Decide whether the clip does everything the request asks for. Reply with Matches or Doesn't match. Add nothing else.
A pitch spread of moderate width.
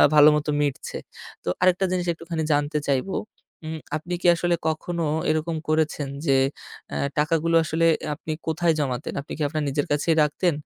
Doesn't match